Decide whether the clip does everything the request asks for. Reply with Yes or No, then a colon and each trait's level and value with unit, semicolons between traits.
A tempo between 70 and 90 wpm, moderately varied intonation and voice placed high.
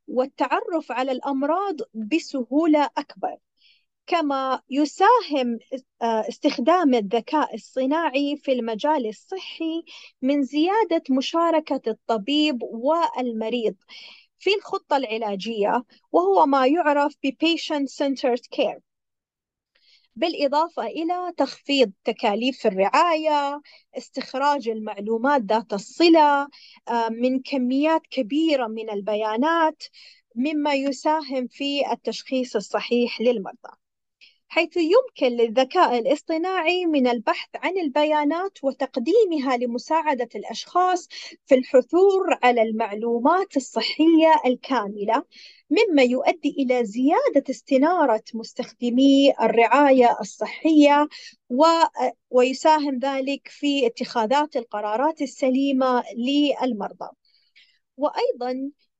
Yes: average, 80 wpm; average, 4.4 semitones; very high, 275 Hz